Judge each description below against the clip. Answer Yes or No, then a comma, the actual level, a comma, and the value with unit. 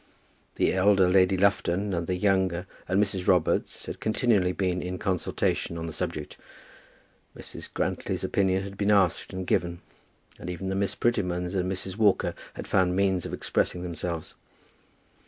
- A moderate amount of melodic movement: No, narrow, 1.6 semitones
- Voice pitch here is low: Yes, very low, 95 Hz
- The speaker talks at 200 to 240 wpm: No, average, 155 wpm